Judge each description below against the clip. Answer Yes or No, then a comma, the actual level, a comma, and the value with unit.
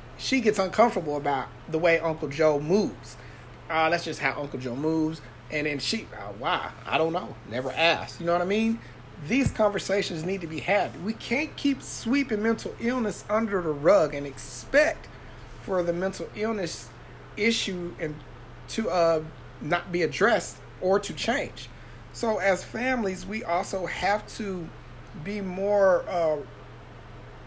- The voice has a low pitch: No, medium, 175 Hz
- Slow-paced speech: No, average, 155 wpm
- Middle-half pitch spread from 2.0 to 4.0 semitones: No, wide, 5.5 semitones